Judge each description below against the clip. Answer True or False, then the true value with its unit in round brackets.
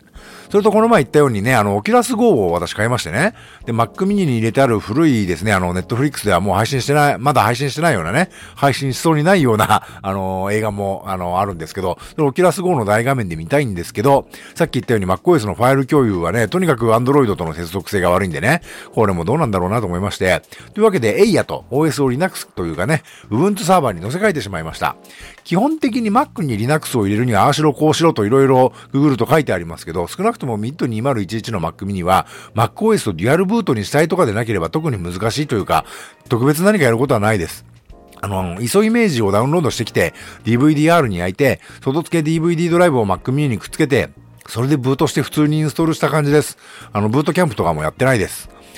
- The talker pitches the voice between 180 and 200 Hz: False (125 Hz)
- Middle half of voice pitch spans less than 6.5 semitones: False (7.5 semitones)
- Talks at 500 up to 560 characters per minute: True (535 characters per minute)